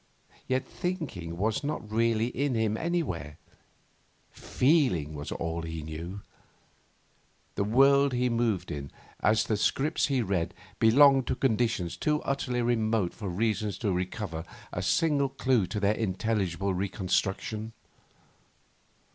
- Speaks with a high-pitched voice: No, low, 110 Hz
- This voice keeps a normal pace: No, slow, 125 wpm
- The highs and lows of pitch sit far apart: Yes, wide, 5.8 semitones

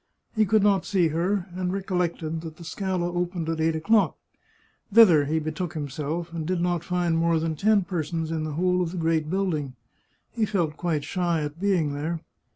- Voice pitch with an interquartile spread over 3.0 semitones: No, narrow, 2.6 semitones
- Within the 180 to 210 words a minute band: Yes, average, 190 wpm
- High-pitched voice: No, medium, 170 Hz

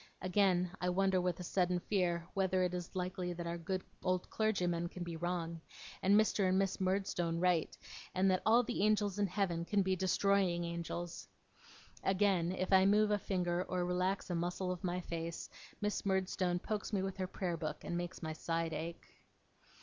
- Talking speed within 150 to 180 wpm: No, average, 190 wpm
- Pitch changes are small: Yes, narrow, 1.9 semitones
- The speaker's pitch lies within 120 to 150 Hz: No, medium, 180 Hz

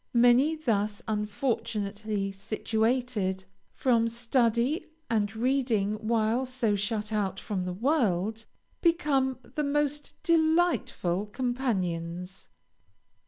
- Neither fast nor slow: No, slow, 90 wpm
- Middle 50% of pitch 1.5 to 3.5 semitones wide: No, average, 4.2 semitones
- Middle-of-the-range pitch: No, high, 225 Hz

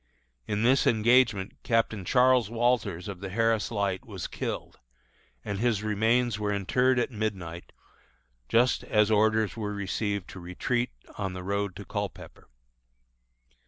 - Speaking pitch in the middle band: No, low, 105 Hz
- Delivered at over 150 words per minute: No, slow, 135 wpm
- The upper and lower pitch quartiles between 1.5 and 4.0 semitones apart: Yes, average, 2.9 semitones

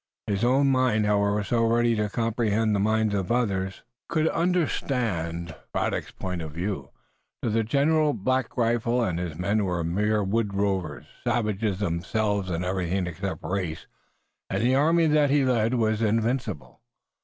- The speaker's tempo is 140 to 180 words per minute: Yes, average, 155 wpm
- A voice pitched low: Yes, low, 110 Hz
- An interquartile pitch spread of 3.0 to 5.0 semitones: Yes, average, 4.0 semitones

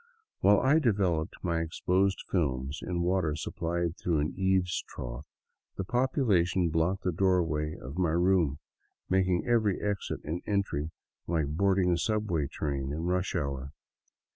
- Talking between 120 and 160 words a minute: Yes, average, 145 wpm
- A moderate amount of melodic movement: Yes, average, 3.5 semitones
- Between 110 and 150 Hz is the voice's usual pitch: No, very low, 90 Hz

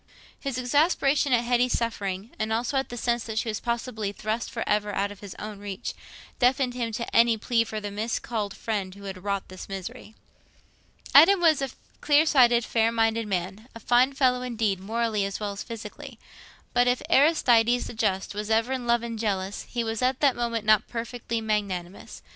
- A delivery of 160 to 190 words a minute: Yes, average, 185 wpm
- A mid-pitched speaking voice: No, high, 230 Hz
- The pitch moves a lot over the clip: No, average, 3.0 semitones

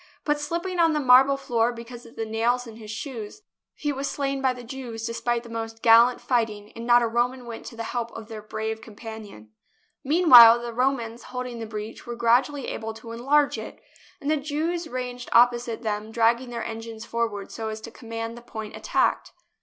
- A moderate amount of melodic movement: No, narrow, 2.2 semitones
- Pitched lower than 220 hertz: No, high, 235 Hz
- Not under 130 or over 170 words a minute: No, average, 200 wpm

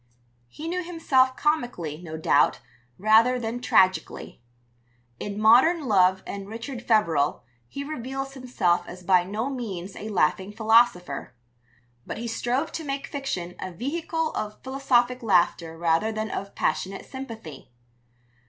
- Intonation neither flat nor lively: No, wide, 6.1 semitones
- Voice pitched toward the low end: No, high, 225 Hz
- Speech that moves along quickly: No, slow, 135 wpm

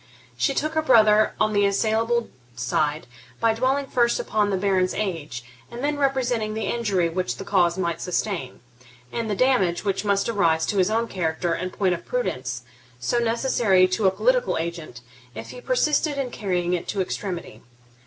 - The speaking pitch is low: No, high, 200 Hz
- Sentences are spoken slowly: No, average, 175 wpm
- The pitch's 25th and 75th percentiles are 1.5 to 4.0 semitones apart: No, average, 5.1 semitones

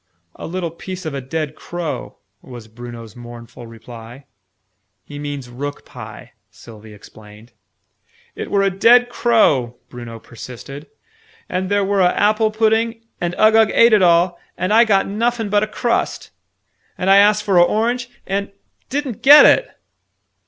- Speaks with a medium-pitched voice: Yes, medium, 180 Hz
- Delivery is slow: No, average, 150 wpm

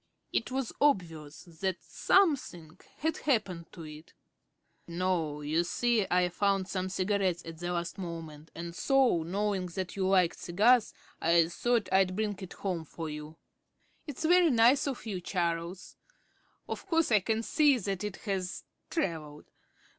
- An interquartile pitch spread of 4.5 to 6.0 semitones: Yes, average, 4.8 semitones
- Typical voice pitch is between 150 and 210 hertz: Yes, medium, 185 Hz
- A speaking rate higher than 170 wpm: No, average, 150 wpm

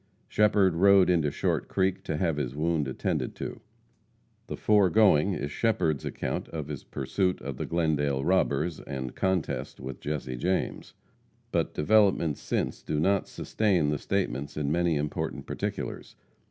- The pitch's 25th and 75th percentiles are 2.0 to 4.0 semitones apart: No, average, 4.6 semitones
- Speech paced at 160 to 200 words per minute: No, average, 145 wpm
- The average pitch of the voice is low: Yes, very low, 80 Hz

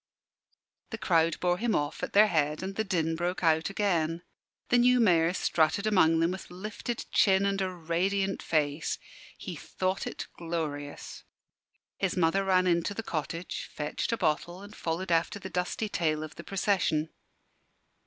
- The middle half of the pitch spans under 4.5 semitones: Yes, average, 3.3 semitones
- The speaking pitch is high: No, medium, 180 Hz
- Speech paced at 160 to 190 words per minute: Yes, average, 165 wpm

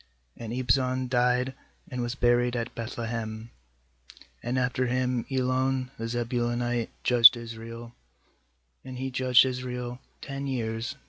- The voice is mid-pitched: No, low, 125 Hz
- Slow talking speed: Yes, slow, 125 wpm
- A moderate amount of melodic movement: No, narrow, 1.5 semitones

